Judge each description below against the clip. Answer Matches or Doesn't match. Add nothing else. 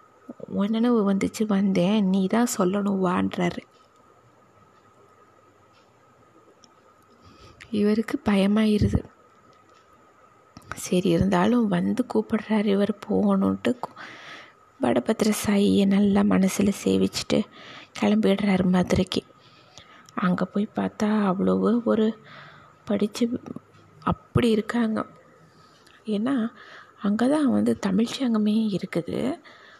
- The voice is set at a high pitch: Matches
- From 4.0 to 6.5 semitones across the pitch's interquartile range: Doesn't match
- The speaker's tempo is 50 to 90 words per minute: Matches